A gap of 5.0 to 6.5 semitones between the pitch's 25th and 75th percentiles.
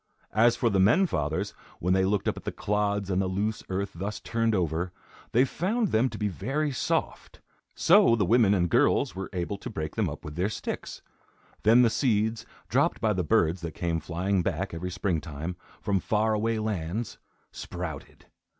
No: average, 3.9 semitones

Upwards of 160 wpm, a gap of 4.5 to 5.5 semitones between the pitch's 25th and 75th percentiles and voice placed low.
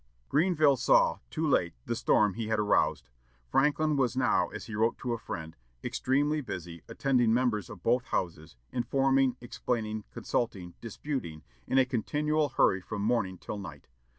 No: average, 155 wpm; average, 4.9 semitones; low, 120 Hz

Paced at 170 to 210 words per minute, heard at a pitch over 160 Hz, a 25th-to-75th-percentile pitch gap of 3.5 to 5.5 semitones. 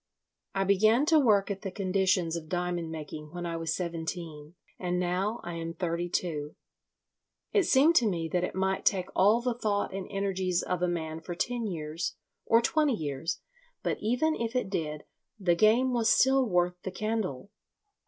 Yes: average, 180 wpm; medium, 185 Hz; average, 4.4 semitones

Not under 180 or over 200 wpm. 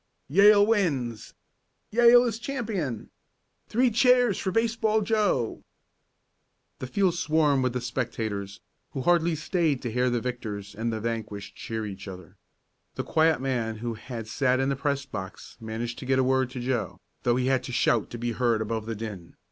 No: average, 170 wpm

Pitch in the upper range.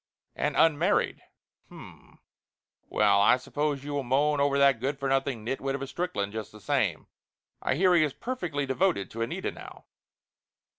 No: medium, 140 Hz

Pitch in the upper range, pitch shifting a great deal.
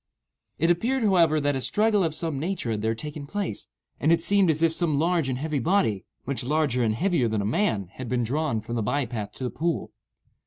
No: medium, 150 Hz; wide, 6.1 semitones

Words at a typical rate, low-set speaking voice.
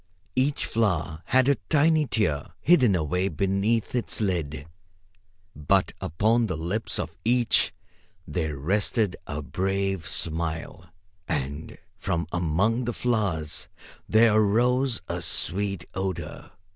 No: slow, 115 wpm; very low, 95 Hz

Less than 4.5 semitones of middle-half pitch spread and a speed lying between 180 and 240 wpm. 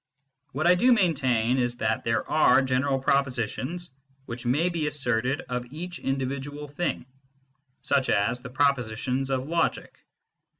No: average, 3.1 semitones; slow, 135 wpm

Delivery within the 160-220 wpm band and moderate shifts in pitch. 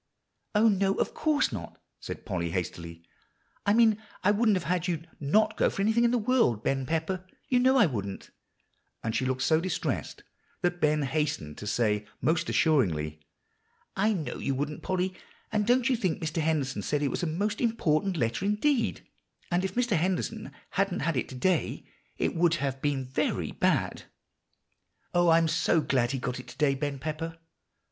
No: average, 185 wpm; wide, 6.9 semitones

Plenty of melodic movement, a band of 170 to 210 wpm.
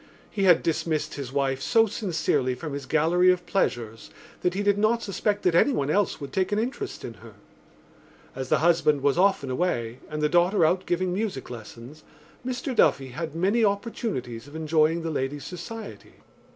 Yes: wide, 6.1 semitones; average, 180 wpm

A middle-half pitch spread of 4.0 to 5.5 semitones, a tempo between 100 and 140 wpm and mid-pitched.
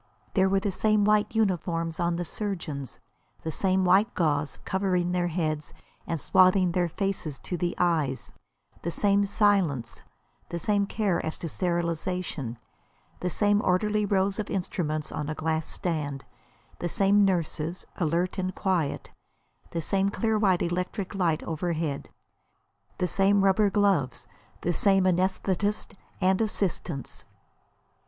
No: average, 3.3 semitones; slow, 135 wpm; medium, 180 Hz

